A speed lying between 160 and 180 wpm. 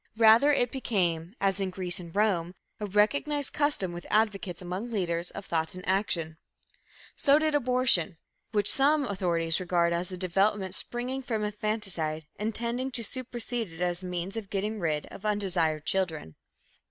Yes: average, 165 wpm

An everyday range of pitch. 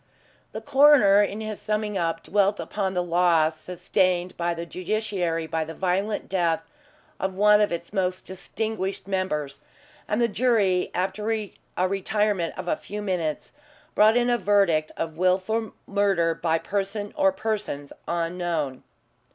Yes: average, 3.5 semitones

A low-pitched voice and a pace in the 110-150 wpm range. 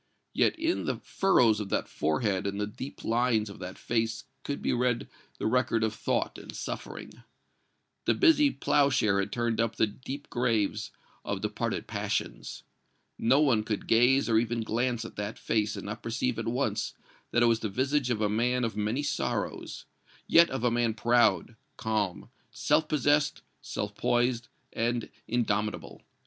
No: low, 115 Hz; average, 165 wpm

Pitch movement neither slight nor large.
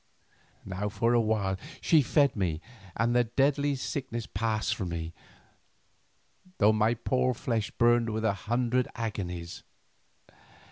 Yes: average, 3.0 semitones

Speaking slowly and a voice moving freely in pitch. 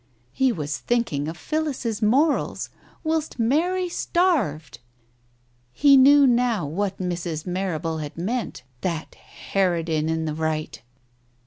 Yes: slow, 115 wpm; wide, 8.8 semitones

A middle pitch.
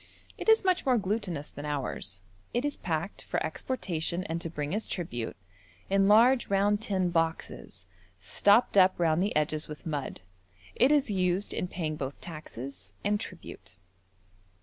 Yes: medium, 175 Hz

